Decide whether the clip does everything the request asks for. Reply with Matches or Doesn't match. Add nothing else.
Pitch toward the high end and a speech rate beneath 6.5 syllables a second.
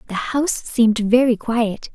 Matches